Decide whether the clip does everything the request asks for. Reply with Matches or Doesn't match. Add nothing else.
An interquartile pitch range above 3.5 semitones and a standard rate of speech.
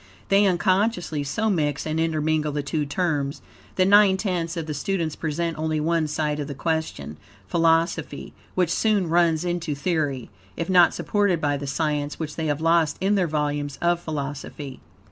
Doesn't match